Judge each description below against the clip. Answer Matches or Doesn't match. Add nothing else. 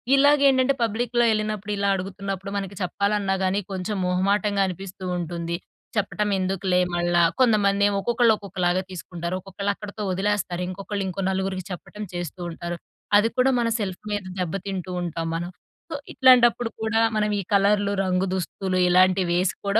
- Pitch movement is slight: Matches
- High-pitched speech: Matches